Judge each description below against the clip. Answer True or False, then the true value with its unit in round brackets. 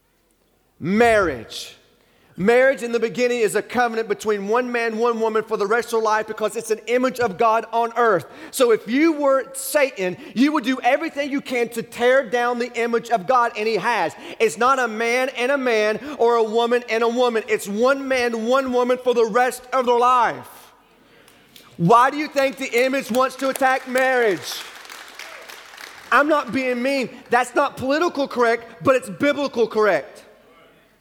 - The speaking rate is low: False (180 wpm)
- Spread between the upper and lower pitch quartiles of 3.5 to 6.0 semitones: False (2.6 semitones)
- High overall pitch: True (245 Hz)